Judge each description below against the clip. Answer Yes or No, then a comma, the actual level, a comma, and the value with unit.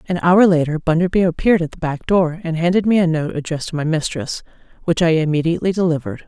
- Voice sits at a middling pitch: Yes, medium, 165 Hz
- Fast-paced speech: Yes, fast, 210 wpm